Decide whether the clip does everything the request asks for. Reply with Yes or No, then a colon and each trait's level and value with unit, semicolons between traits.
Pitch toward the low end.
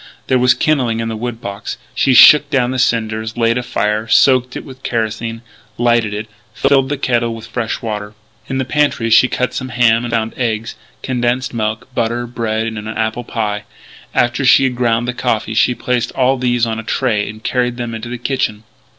Yes: low, 120 Hz